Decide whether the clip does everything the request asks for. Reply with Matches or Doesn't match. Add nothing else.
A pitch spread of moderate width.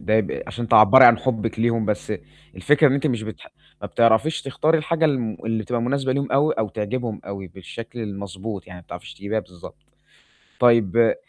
Matches